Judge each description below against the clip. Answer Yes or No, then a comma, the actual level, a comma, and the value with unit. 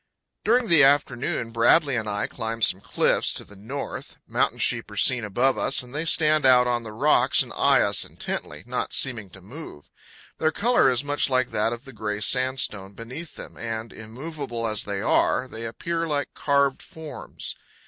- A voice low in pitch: Yes, low, 125 Hz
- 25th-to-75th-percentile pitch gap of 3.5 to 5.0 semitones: Yes, average, 4.5 semitones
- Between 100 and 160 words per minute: No, average, 185 wpm